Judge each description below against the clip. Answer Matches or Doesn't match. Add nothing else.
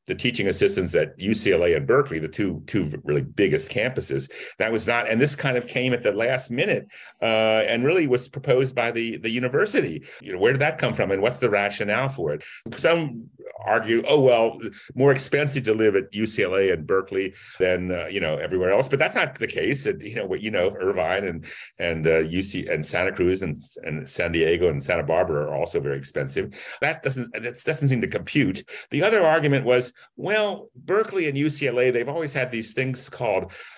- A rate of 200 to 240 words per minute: Matches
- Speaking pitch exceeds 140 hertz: Doesn't match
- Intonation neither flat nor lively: Matches